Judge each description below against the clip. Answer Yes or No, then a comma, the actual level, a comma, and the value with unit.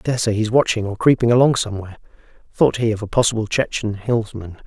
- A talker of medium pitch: No, low, 110 Hz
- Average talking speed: Yes, average, 195 wpm